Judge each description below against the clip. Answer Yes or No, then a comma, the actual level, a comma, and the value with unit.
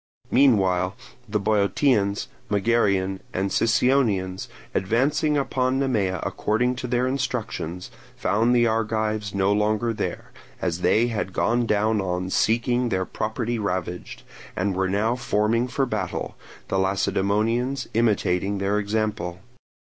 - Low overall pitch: Yes, low, 105 Hz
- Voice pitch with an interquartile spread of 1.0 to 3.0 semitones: No, average, 3.6 semitones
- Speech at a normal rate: No, slow, 120 wpm